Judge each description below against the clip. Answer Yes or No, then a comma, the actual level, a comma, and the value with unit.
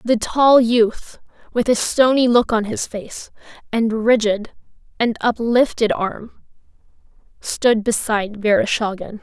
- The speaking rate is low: Yes, slow, 115 wpm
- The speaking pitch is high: Yes, high, 225 Hz